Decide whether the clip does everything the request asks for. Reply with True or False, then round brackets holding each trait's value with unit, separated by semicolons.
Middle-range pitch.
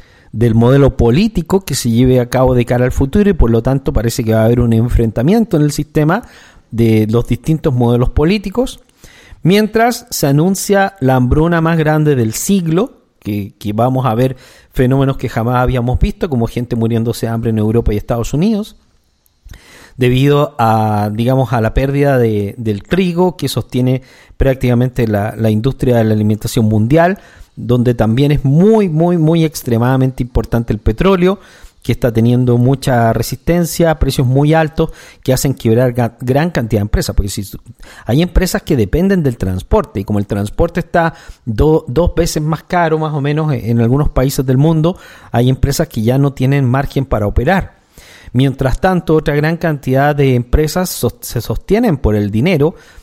False (130 Hz)